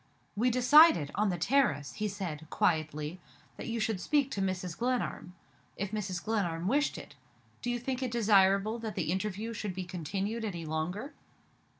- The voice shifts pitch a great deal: No, average, 4.7 semitones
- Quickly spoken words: No, average, 170 wpm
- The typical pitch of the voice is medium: No, high, 205 Hz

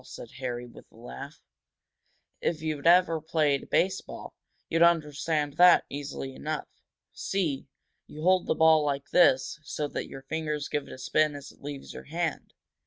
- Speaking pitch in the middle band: Yes, medium, 150 Hz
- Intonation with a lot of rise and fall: No, average, 2.8 semitones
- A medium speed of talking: Yes, average, 165 wpm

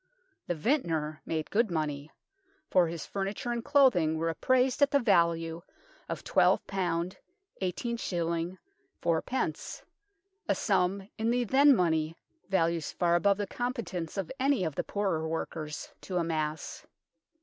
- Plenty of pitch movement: Yes, wide, 6.2 semitones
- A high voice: No, medium, 180 Hz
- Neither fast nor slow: No, slow, 130 wpm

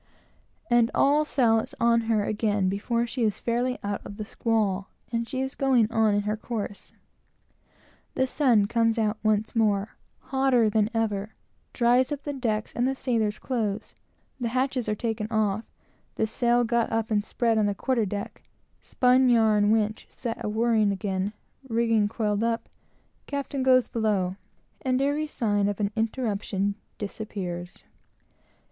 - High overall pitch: Yes, high, 225 Hz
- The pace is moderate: Yes, average, 160 wpm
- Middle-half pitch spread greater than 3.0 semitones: No, average, 2.7 semitones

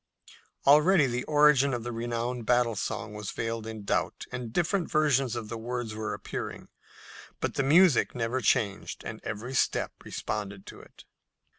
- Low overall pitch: Yes, low, 120 Hz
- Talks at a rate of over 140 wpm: Yes, average, 160 wpm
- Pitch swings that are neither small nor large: Yes, average, 3.6 semitones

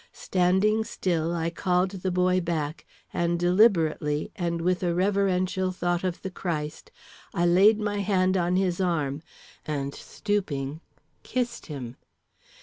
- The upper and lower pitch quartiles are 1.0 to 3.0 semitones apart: Yes, narrow, 2.4 semitones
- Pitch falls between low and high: Yes, medium, 180 Hz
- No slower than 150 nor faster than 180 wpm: No, slow, 135 wpm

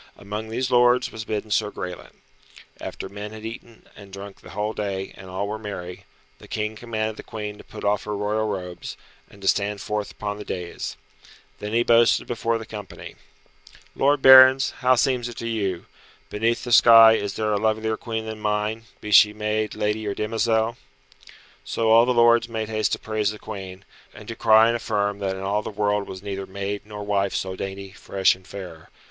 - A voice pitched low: Yes, low, 105 Hz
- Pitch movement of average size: No, narrow, 1.9 semitones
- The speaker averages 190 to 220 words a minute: Yes, average, 200 wpm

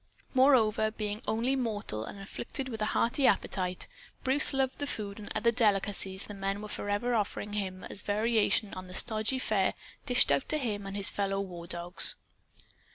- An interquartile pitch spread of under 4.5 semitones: Yes, average, 3.3 semitones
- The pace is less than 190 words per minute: Yes, average, 180 wpm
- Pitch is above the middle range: Yes, high, 210 Hz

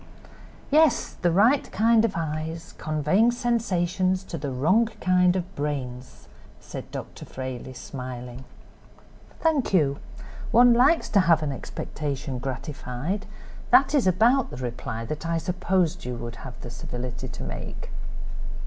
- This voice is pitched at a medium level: Yes, medium, 165 Hz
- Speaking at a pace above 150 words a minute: No, slow, 135 wpm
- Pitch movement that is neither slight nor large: No, wide, 7.7 semitones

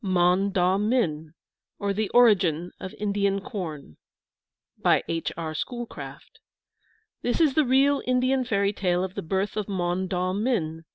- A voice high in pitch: Yes, high, 195 Hz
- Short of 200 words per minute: Yes, average, 150 wpm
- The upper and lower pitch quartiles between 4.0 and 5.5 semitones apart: Yes, average, 4.4 semitones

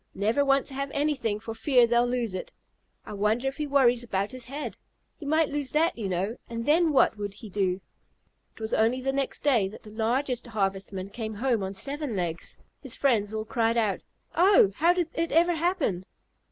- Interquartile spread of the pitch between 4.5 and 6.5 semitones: Yes, average, 5.2 semitones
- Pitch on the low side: No, high, 235 Hz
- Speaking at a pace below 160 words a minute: No, fast, 205 wpm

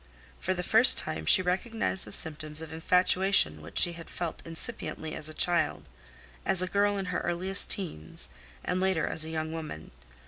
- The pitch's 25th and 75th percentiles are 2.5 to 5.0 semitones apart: Yes, average, 3.1 semitones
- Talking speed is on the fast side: No, average, 180 wpm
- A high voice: No, medium, 175 Hz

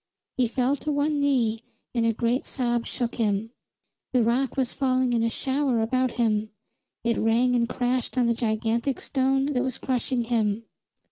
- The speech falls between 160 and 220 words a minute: Yes, average, 175 wpm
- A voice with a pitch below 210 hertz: No, high, 245 Hz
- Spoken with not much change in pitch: Yes, narrow, 2.2 semitones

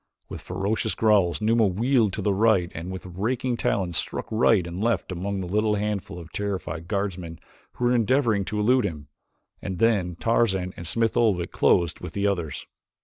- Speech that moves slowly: No, average, 180 wpm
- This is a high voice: No, low, 100 Hz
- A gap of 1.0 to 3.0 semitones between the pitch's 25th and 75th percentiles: No, average, 3.8 semitones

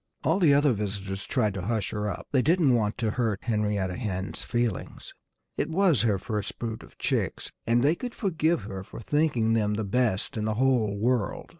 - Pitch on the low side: Yes, low, 110 Hz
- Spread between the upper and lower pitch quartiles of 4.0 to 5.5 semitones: Yes, average, 4.3 semitones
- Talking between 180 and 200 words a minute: Yes, average, 195 wpm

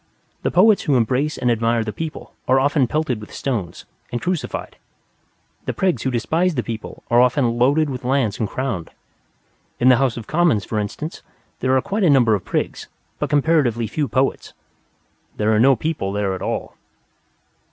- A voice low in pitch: Yes, low, 130 Hz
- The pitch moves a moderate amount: Yes, average, 4.7 semitones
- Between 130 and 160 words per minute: No, average, 180 wpm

